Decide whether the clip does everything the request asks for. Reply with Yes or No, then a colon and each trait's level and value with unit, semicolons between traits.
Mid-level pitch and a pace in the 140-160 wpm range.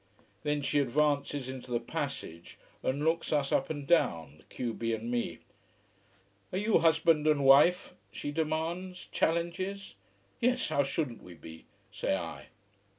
Yes: medium, 145 Hz; average, 150 wpm